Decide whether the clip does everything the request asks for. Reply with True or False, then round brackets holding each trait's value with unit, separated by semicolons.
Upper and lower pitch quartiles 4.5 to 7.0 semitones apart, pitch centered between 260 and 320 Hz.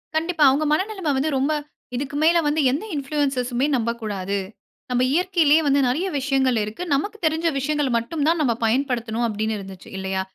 True (4.9 semitones; 275 Hz)